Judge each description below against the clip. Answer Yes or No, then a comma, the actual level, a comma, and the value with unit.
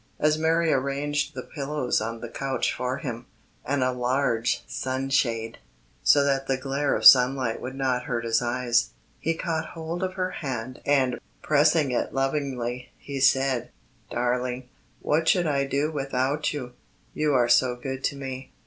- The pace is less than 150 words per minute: No, average, 160 wpm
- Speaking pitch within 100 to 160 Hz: Yes, low, 135 Hz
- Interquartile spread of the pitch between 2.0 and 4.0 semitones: Yes, average, 2.7 semitones